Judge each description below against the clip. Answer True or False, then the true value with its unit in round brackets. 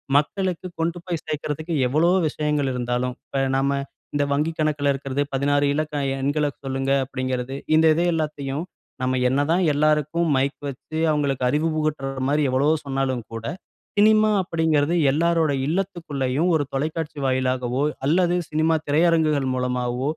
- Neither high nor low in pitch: True (145 Hz)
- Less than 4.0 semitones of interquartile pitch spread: True (3.0 semitones)